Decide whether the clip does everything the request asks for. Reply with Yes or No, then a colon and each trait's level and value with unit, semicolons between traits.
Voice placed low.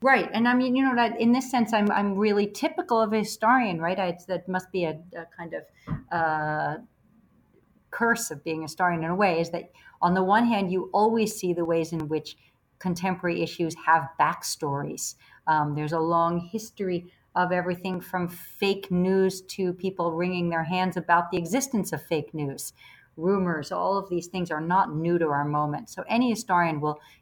No: medium, 180 Hz